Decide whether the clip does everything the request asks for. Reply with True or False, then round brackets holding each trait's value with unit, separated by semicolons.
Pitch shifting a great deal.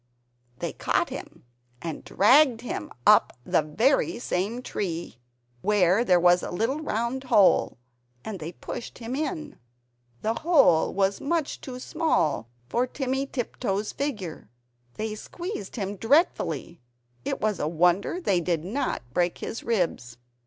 True (6.9 semitones)